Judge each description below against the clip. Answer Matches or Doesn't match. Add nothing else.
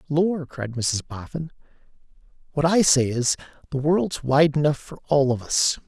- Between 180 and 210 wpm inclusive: Doesn't match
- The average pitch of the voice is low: Doesn't match